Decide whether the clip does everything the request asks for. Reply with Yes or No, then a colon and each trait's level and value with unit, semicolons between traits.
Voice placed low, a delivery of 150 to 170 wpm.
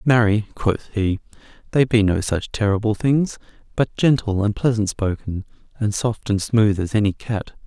Yes: low, 110 Hz; average, 165 wpm